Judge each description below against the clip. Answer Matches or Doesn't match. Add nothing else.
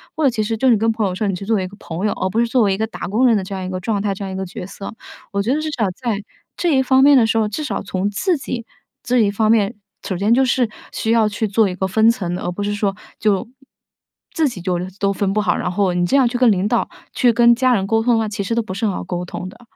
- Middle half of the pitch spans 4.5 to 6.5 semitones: Doesn't match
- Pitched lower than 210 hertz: Doesn't match